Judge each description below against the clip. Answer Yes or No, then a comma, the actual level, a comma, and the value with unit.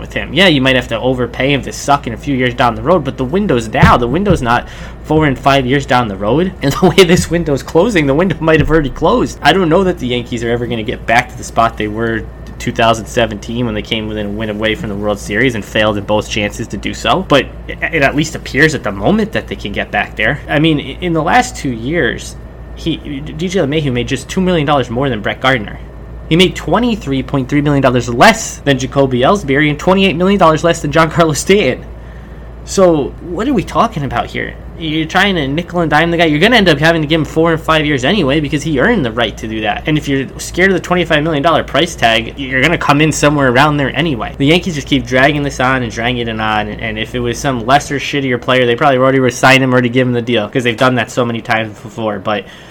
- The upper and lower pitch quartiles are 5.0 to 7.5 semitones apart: Yes, average, 5.3 semitones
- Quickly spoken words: Yes, fast, 260 wpm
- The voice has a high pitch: No, low, 135 Hz